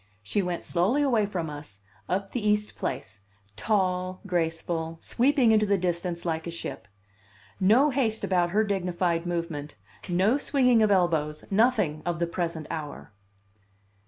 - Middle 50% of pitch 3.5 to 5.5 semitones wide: Yes, average, 4.1 semitones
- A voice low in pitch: No, medium, 180 Hz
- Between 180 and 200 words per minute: No, average, 145 wpm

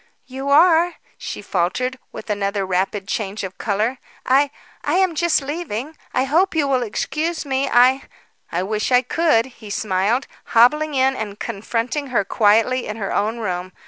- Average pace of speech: Yes, average, 170 wpm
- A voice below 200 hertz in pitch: No, very high, 250 Hz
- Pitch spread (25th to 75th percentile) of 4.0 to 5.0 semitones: No, wide, 5.5 semitones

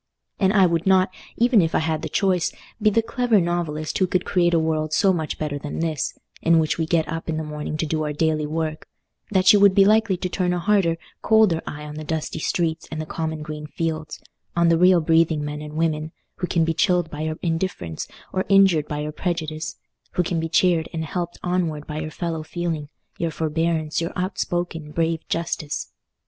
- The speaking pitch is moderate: Yes, medium, 165 Hz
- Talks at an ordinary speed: No, fast, 210 wpm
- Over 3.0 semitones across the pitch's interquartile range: No, narrow, 2.4 semitones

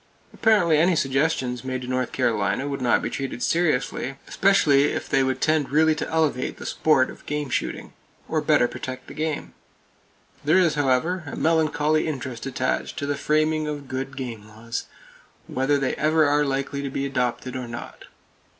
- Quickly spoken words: No, average, 175 wpm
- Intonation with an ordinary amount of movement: Yes, average, 3.1 semitones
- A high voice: No, medium, 140 Hz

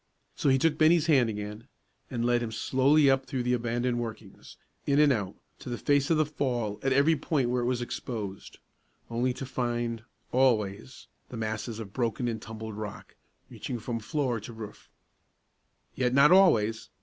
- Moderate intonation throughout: Yes, average, 3.2 semitones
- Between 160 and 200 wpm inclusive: Yes, average, 175 wpm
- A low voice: Yes, low, 120 Hz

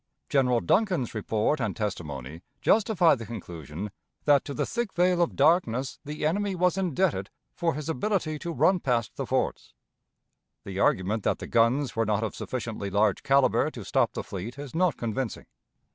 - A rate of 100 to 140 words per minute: No, average, 170 wpm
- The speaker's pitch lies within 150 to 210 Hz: No, low, 130 Hz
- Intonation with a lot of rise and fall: Yes, wide, 7.9 semitones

